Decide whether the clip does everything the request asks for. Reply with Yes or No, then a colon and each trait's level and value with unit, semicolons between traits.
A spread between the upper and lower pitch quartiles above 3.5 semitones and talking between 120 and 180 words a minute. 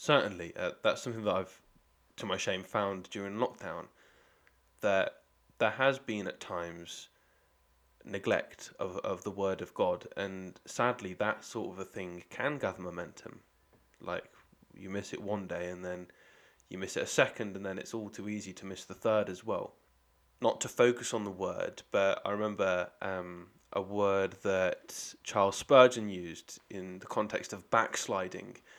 No: average, 2.9 semitones; average, 170 wpm